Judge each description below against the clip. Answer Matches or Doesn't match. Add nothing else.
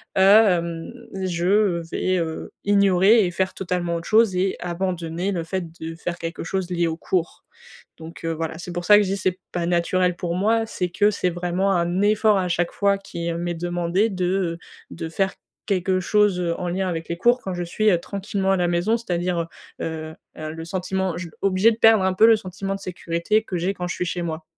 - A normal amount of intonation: Doesn't match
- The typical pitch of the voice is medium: Matches